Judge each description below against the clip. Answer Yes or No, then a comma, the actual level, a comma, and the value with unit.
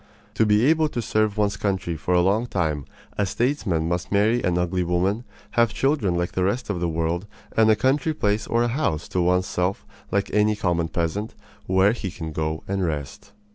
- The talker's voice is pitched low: Yes, low, 100 Hz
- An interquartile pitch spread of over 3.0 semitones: Yes, average, 3.9 semitones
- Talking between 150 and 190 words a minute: No, fast, 205 wpm